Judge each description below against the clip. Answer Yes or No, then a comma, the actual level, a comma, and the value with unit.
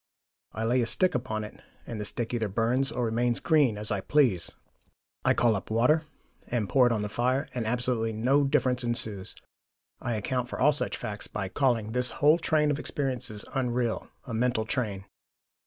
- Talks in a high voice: No, low, 120 Hz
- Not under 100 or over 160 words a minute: No, average, 190 wpm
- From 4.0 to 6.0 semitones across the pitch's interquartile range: No, average, 2.8 semitones